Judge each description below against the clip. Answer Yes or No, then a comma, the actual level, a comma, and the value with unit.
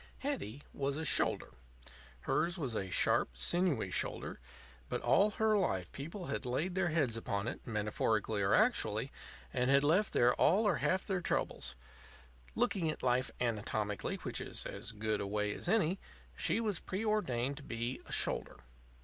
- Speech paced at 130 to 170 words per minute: Yes, average, 165 wpm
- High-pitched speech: No, medium, 140 Hz